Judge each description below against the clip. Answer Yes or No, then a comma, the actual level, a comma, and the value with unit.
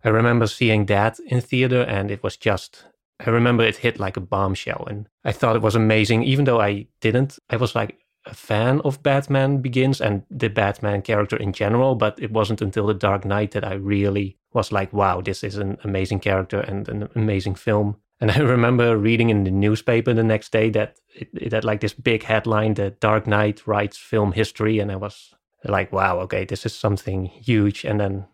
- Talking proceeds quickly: Yes, fast, 210 wpm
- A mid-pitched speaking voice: No, low, 110 Hz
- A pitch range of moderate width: No, narrow, 2.2 semitones